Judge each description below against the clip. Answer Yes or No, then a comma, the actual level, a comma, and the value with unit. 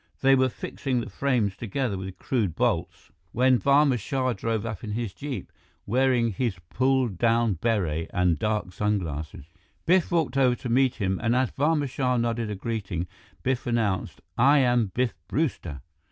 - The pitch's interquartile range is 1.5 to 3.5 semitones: No, average, 4.5 semitones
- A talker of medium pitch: No, low, 120 Hz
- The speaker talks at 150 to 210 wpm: Yes, average, 170 wpm